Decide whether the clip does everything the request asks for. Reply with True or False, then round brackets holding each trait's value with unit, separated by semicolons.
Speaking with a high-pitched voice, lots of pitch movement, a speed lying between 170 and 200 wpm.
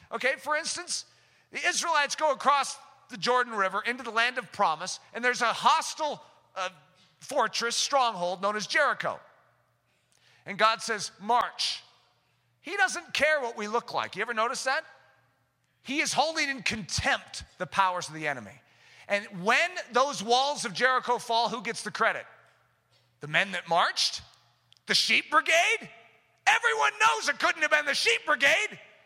False (235 Hz; 7.3 semitones; 160 wpm)